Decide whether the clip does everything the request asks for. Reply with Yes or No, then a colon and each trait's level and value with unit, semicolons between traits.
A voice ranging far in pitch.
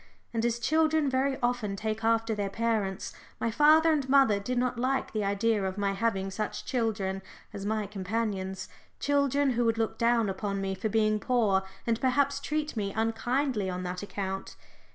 No: average, 4.2 semitones